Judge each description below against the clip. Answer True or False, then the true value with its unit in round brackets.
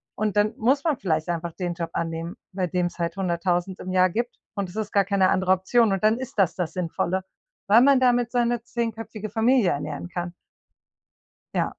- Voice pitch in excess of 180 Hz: True (190 Hz)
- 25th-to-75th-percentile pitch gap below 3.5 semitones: False (4.4 semitones)